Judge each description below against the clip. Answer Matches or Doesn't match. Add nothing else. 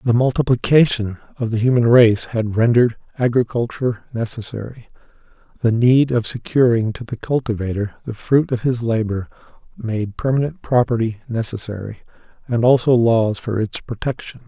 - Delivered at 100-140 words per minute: Matches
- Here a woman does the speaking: Doesn't match